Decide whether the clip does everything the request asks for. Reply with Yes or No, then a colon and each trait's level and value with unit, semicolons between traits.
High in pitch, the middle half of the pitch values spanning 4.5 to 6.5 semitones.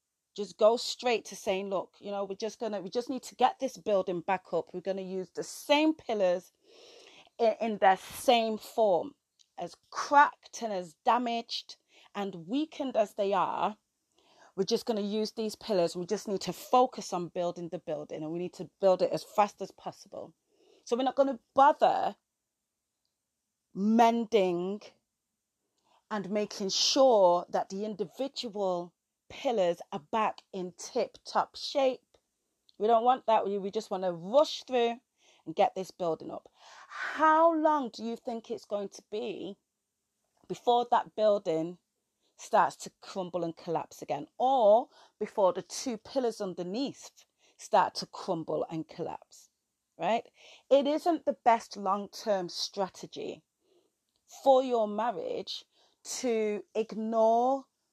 Yes: high, 215 Hz; average, 5.1 semitones